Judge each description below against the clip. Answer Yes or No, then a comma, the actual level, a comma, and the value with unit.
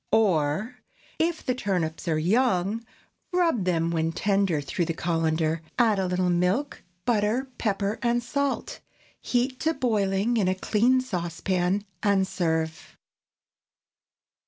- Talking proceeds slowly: Yes, slow, 125 wpm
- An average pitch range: No, wide, 5.7 semitones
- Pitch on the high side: Yes, high, 195 Hz